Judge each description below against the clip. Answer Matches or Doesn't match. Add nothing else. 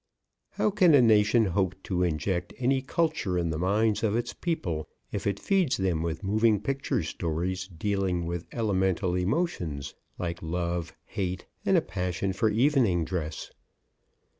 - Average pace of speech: Matches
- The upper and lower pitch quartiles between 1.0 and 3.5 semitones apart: Doesn't match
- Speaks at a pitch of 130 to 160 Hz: Doesn't match